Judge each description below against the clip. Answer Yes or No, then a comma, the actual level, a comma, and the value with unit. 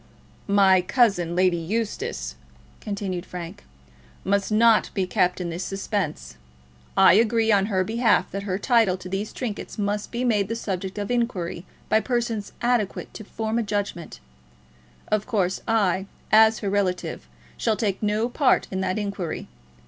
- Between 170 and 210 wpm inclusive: No, average, 155 wpm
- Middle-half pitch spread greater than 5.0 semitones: No, average, 3.1 semitones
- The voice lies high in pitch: Yes, high, 205 Hz